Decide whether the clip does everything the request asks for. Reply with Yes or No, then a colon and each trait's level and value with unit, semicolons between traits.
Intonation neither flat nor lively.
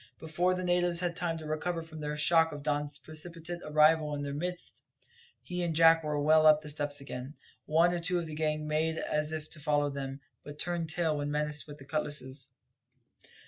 No: narrow, 2.0 semitones